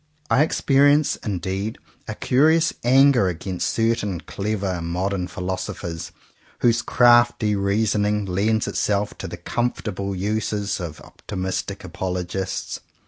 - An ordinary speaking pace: No, slow, 105 wpm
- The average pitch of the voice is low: Yes, low, 100 Hz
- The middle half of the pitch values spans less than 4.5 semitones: Yes, average, 3.8 semitones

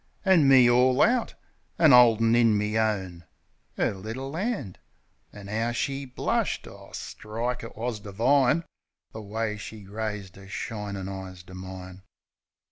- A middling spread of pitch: Yes, average, 4.0 semitones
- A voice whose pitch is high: No, low, 110 Hz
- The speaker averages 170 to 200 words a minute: No, average, 140 wpm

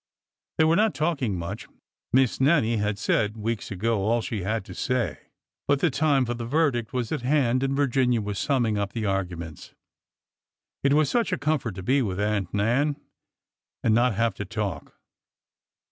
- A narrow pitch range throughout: No, average, 5.0 semitones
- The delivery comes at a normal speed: Yes, average, 175 wpm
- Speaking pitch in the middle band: No, low, 115 Hz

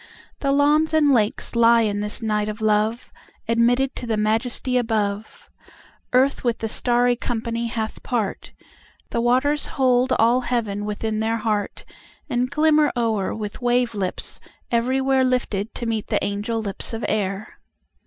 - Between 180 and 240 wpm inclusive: No, slow, 135 wpm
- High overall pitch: Yes, high, 230 Hz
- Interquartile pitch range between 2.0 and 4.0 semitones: Yes, average, 2.8 semitones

